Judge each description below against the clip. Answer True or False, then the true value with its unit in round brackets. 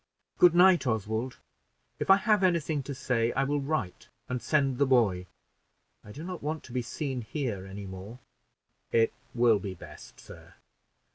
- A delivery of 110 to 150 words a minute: False (170 wpm)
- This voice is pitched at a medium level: False (130 Hz)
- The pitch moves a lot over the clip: True (5.7 semitones)